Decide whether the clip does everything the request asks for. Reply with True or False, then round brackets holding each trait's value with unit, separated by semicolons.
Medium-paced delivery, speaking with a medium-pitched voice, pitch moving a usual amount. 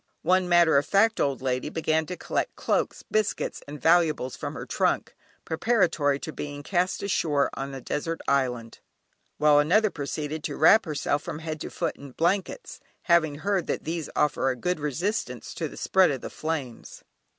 True (175 wpm; 155 Hz; 3.7 semitones)